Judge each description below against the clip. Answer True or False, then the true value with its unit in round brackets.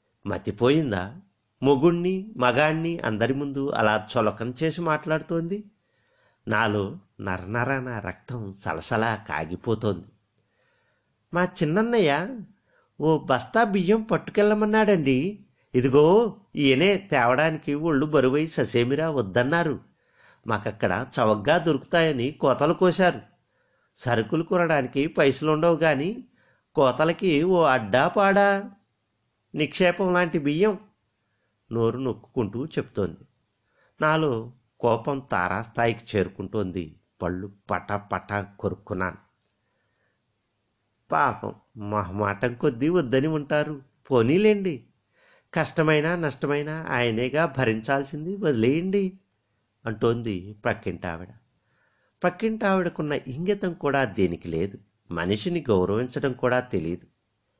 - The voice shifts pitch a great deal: True (7.6 semitones)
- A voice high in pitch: False (135 Hz)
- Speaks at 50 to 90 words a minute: True (80 wpm)